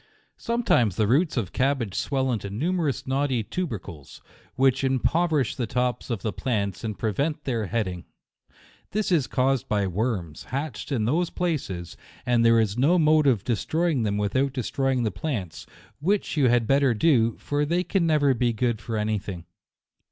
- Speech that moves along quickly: No, average, 175 wpm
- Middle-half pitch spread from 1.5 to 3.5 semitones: No, average, 5.3 semitones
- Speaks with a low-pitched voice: Yes, low, 125 Hz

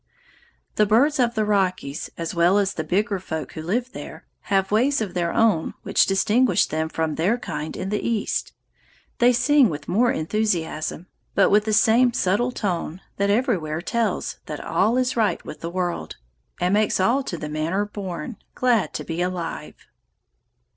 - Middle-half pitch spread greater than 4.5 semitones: Yes, average, 5.1 semitones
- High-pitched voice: Yes, high, 200 Hz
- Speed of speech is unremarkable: Yes, average, 175 wpm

